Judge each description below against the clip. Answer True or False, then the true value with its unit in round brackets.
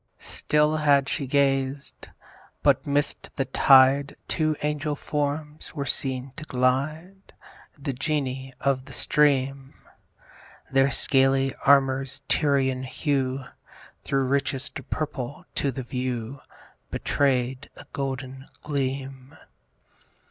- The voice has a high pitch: False (135 Hz)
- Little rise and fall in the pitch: True (1.6 semitones)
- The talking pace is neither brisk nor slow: False (105 wpm)